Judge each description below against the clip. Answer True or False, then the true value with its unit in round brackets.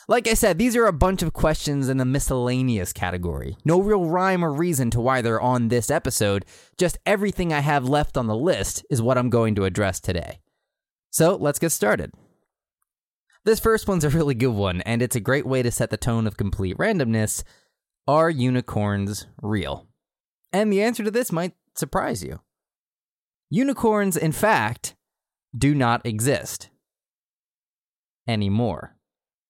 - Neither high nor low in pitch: False (130 Hz)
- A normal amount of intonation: False (8.0 semitones)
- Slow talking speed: False (165 wpm)